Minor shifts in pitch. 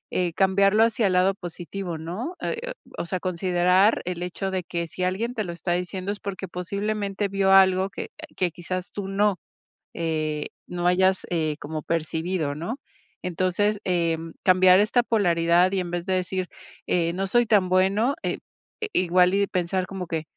Yes: narrow, 2.2 semitones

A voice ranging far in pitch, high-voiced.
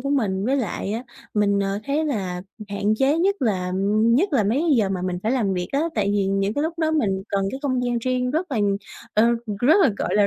Yes: wide, 5.9 semitones; high, 230 Hz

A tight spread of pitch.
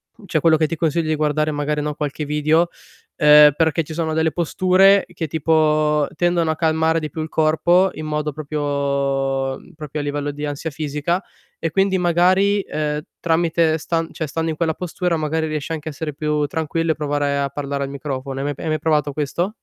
Yes: narrow, 1.9 semitones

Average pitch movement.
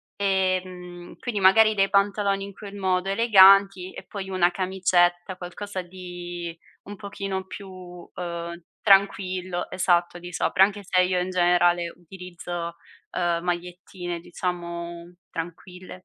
No: narrow, 1.7 semitones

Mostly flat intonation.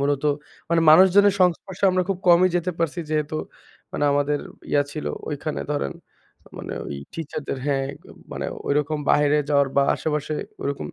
No: average, 3.2 semitones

